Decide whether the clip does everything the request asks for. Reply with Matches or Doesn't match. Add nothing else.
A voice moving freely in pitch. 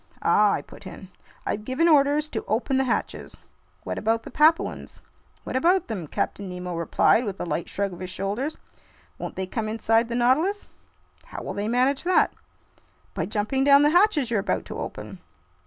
Matches